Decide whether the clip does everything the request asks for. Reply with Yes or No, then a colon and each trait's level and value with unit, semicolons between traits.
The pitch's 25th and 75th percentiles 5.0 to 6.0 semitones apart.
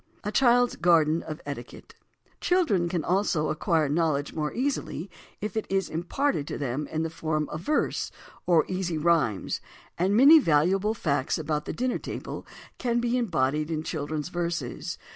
Yes: wide, 5.4 semitones